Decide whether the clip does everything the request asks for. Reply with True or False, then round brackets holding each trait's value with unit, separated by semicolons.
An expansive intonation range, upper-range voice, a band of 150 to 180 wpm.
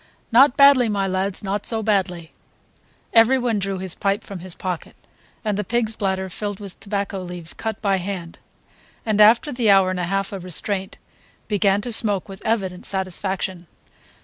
False (2.5 semitones; 195 Hz; 170 wpm)